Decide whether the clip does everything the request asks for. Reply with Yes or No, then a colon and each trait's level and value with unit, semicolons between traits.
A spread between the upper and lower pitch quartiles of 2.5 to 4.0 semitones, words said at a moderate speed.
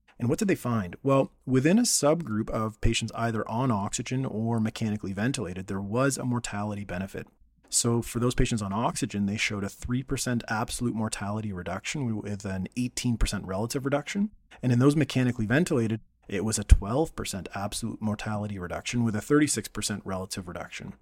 Yes: average, 3.7 semitones; average, 165 wpm